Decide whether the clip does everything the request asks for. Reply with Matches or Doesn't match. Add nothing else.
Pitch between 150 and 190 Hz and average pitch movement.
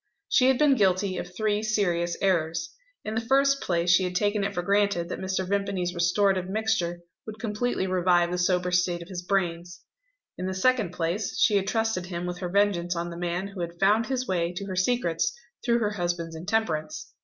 Matches